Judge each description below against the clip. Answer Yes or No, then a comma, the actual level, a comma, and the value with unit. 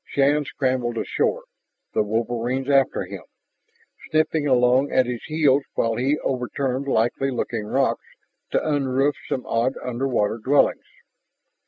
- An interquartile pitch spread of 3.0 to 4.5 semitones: No, narrow, 2.6 semitones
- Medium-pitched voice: No, low, 130 Hz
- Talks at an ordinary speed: No, slow, 125 wpm